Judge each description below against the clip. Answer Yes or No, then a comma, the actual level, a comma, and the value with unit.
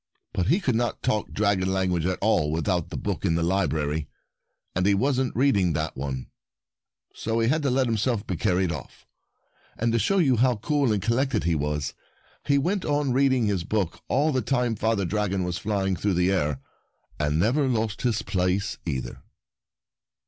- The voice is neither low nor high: No, low, 105 Hz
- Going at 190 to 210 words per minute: Yes, average, 200 wpm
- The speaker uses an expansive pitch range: Yes, wide, 5.9 semitones